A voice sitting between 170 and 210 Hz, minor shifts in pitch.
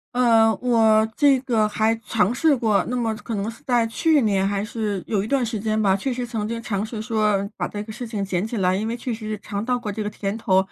No: high, 220 Hz; narrow, 2.3 semitones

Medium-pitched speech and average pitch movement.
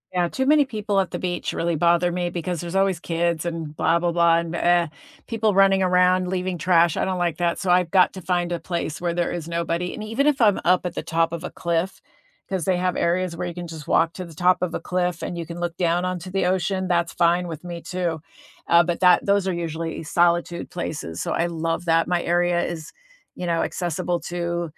No: medium, 175 Hz; narrow, 1.3 semitones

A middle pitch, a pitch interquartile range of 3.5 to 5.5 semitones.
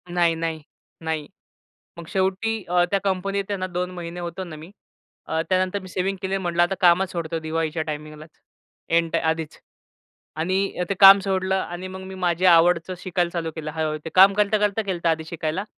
No: medium, 175 Hz; narrow, 2.6 semitones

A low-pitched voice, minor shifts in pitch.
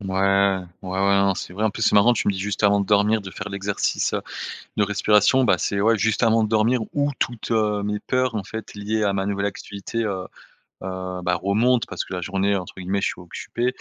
Yes: low, 100 Hz; narrow, 2.1 semitones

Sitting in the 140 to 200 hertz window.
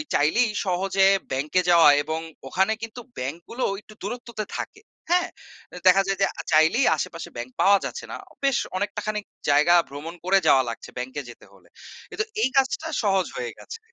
Yes: high, 190 Hz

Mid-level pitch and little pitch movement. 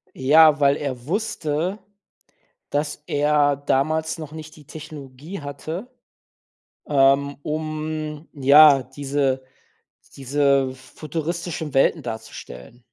Yes: medium, 145 Hz; narrow, 2.3 semitones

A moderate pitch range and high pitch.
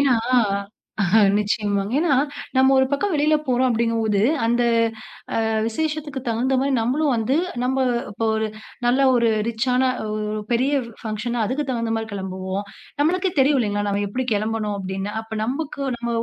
Yes: average, 3.7 semitones; high, 235 Hz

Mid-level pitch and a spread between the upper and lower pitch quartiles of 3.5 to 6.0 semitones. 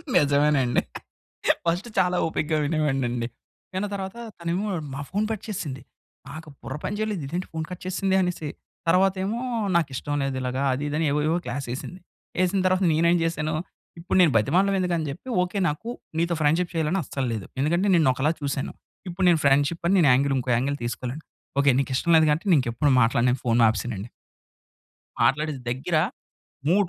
Yes: medium, 155 Hz; average, 4.8 semitones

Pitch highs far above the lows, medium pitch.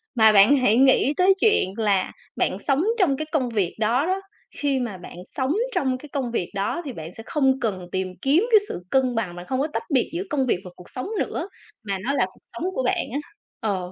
No: wide, 5.7 semitones; very high, 255 Hz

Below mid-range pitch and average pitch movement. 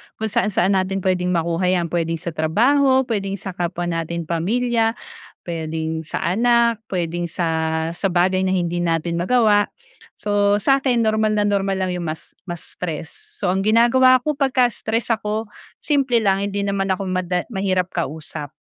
No: high, 190 Hz; average, 4.2 semitones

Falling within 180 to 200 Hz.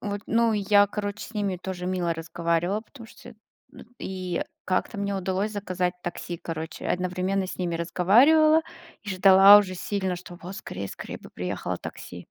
Yes: high, 190 Hz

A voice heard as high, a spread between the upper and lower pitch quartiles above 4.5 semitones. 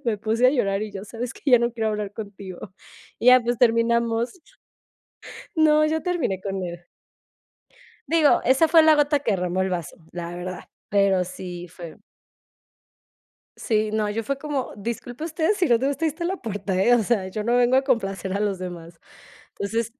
Yes: high, 225 Hz; average, 5.2 semitones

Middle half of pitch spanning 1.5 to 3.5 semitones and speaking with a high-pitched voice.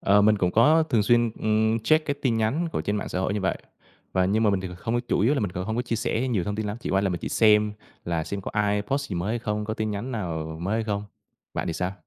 No: average, 2.8 semitones; low, 105 Hz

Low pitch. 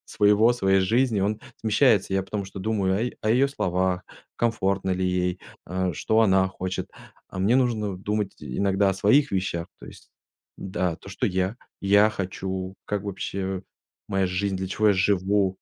Yes: very low, 95 Hz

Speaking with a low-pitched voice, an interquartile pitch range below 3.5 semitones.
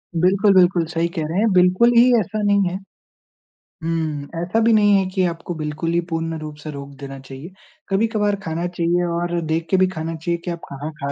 No: medium, 170 Hz; average, 3.0 semitones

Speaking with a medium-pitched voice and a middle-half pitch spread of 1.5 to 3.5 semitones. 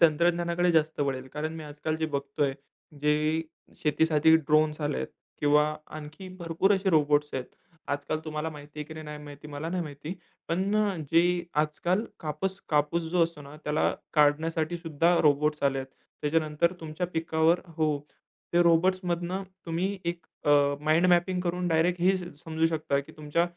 Yes: medium, 160 Hz; narrow, 2.5 semitones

